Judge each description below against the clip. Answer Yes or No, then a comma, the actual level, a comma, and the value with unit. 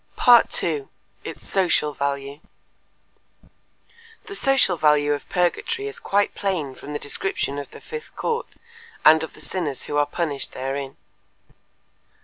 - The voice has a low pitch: No, medium, 150 Hz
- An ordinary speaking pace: No, slow, 130 wpm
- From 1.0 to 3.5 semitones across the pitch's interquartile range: No, average, 5.3 semitones